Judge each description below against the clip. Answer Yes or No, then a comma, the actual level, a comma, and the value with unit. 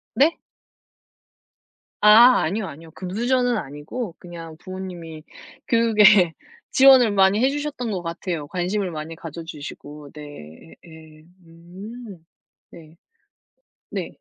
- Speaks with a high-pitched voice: No, medium, 180 Hz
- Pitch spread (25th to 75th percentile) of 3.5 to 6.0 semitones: Yes, wide, 5.4 semitones